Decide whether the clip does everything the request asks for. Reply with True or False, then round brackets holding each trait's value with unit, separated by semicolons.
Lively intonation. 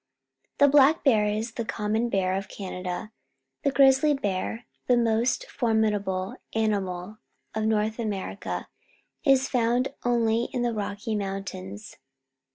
False (3.3 semitones)